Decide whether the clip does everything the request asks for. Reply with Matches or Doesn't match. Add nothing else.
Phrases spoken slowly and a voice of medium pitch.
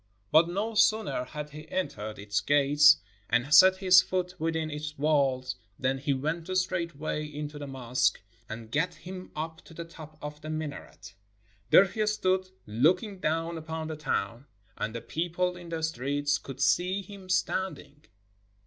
Doesn't match